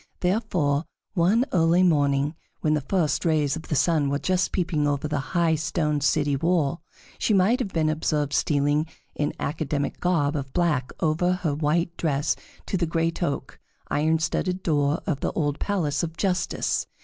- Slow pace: No, average, 170 wpm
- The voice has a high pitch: No, medium, 155 Hz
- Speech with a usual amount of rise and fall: Yes, average, 3.2 semitones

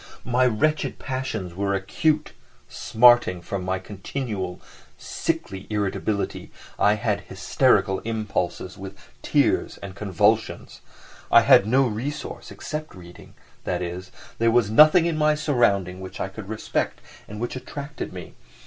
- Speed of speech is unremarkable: No, slow, 130 wpm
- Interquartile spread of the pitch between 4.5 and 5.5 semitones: Yes, average, 5.0 semitones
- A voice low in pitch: Yes, low, 105 Hz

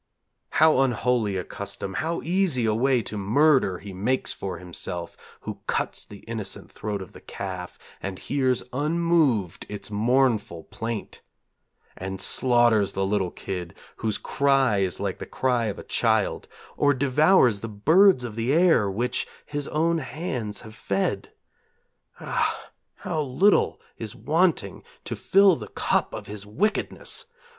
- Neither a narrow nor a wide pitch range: No, wide, 6.1 semitones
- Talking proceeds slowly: No, average, 145 wpm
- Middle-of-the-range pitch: No, low, 115 Hz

